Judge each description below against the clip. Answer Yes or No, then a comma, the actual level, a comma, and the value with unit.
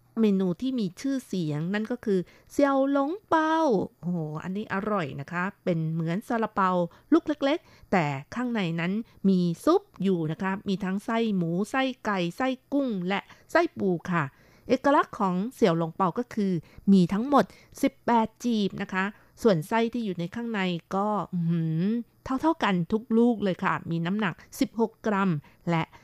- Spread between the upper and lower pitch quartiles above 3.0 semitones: Yes, average, 5.2 semitones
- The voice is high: Yes, high, 200 Hz